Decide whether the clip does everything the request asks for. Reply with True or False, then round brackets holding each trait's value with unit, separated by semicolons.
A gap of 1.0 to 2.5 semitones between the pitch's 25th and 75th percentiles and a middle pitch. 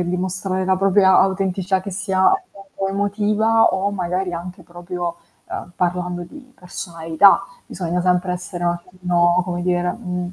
True (1.7 semitones; 180 Hz)